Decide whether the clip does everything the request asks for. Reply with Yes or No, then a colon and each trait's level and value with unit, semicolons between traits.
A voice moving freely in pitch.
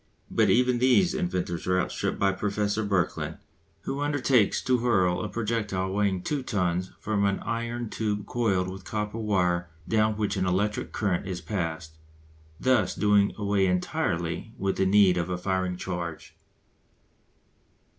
No: average, 3.3 semitones